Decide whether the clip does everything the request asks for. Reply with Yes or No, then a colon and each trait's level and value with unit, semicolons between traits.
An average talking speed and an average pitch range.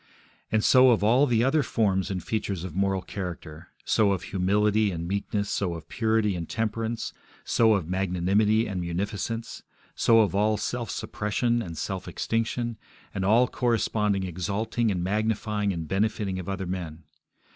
Yes: average, 155 wpm; average, 3.2 semitones